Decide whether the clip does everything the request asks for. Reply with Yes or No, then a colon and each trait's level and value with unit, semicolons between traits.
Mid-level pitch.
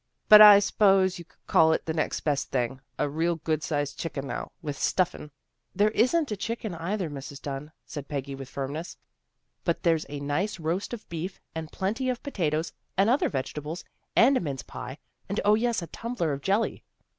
Yes: medium, 165 Hz